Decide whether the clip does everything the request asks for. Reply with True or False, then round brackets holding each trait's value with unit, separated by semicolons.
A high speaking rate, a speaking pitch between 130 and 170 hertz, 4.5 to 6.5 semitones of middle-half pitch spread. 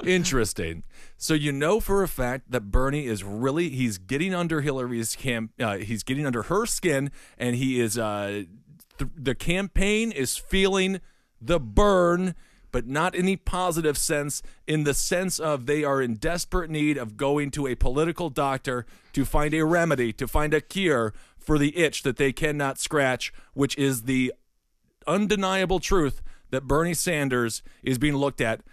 False (170 wpm; 140 Hz; 5.3 semitones)